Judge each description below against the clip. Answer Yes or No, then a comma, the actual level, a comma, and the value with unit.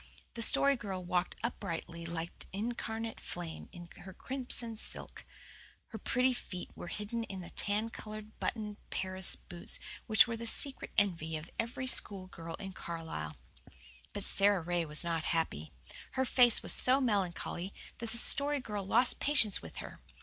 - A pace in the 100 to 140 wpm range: No, average, 165 wpm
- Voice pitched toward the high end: Yes, high, 205 Hz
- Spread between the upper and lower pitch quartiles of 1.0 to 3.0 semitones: No, average, 5.1 semitones